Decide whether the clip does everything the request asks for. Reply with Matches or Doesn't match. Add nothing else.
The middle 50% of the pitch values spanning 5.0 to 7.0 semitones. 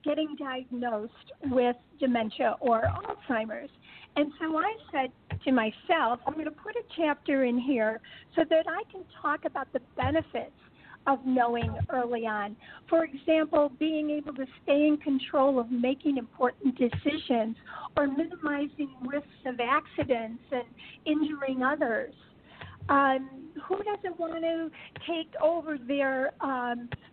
Doesn't match